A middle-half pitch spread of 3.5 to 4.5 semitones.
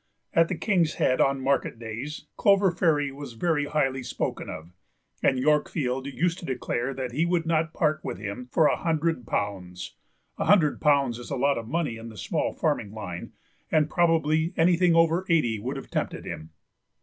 No: average, 5.3 semitones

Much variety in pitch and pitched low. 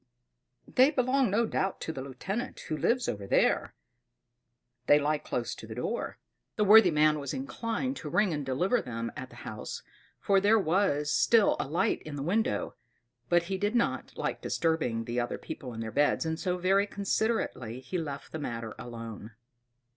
No: wide, 8.0 semitones; medium, 160 Hz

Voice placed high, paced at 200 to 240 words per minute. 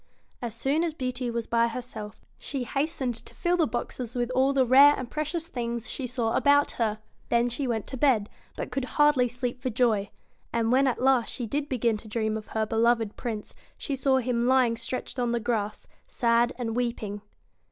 Yes: high, 245 Hz; fast, 205 wpm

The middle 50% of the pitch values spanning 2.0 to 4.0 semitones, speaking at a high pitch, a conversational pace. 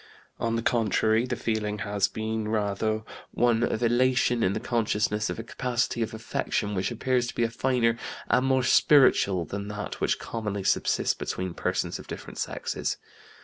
No: narrow, 2.5 semitones; low, 115 Hz; average, 165 wpm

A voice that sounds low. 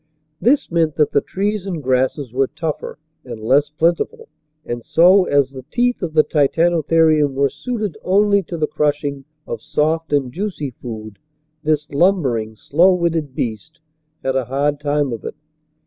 No: medium, 150 Hz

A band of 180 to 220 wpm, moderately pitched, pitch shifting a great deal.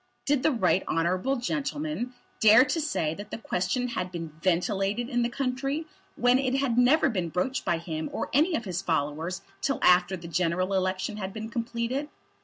No: average, 185 wpm; high, 220 Hz; wide, 6.2 semitones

